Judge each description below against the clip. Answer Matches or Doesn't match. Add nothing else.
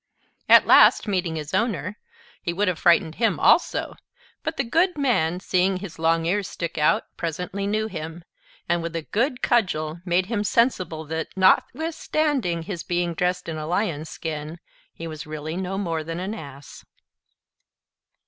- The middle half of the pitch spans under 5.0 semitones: Matches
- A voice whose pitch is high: Doesn't match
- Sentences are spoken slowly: Doesn't match